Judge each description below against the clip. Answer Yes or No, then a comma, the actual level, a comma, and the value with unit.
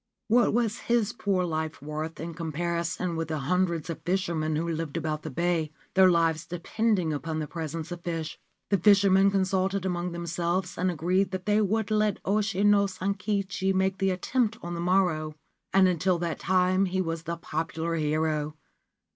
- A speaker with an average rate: Yes, average, 170 wpm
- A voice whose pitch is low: No, medium, 175 Hz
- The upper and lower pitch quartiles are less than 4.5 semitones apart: Yes, average, 2.9 semitones